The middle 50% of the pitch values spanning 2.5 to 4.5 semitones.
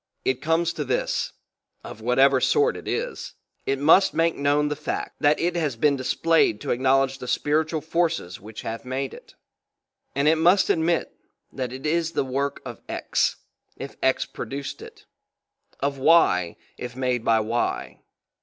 Yes: average, 4.0 semitones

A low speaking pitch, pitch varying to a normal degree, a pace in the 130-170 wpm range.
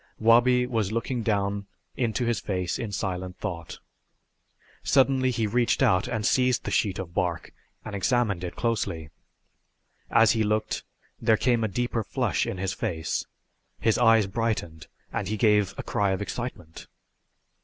Yes: low, 110 Hz; average, 3.7 semitones; average, 155 wpm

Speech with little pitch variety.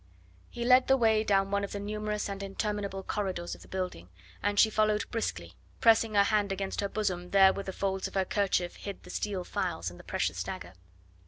Yes: narrow, 1.9 semitones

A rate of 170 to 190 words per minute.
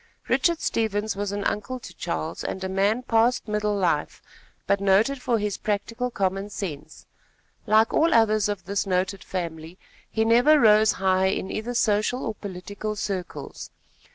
No: average, 155 wpm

